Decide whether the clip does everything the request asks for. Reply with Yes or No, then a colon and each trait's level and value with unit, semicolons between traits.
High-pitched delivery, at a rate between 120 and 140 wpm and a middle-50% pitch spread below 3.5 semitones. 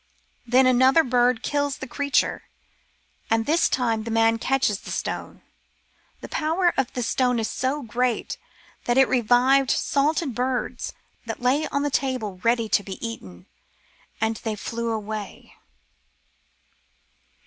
Yes: high, 245 Hz; slow, 135 wpm; average, 3.0 semitones